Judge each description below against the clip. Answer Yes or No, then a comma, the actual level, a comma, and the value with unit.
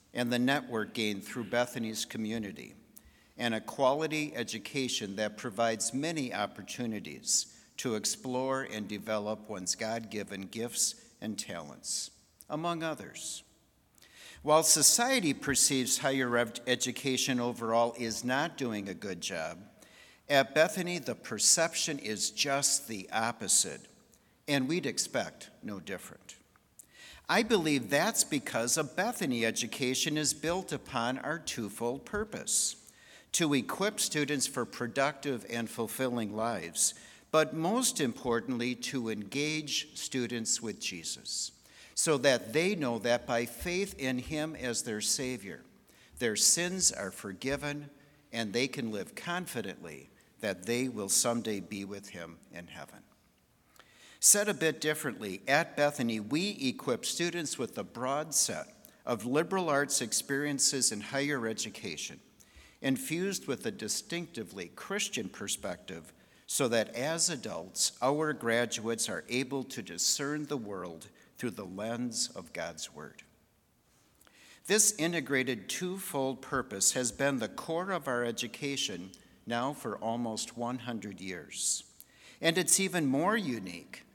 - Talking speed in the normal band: No, slow, 125 wpm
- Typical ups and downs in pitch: Yes, average, 4.9 semitones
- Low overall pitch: Yes, low, 130 Hz